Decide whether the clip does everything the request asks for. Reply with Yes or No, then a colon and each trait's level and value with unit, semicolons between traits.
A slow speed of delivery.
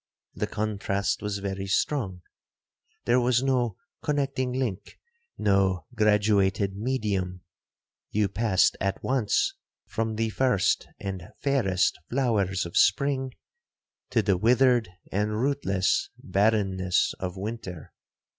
Yes: slow, 105 wpm